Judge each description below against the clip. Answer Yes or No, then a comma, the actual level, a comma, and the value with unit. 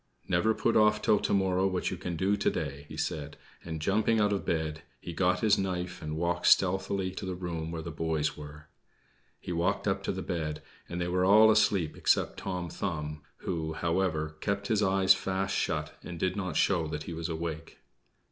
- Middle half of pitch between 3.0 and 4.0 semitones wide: Yes, average, 3.3 semitones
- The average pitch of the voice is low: Yes, very low, 90 Hz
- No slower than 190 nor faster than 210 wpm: Yes, fast, 205 wpm